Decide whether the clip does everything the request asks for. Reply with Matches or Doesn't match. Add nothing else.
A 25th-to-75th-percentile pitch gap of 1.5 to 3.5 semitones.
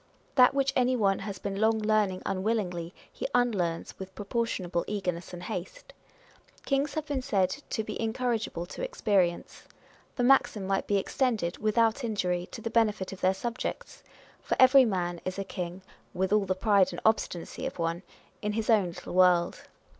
Doesn't match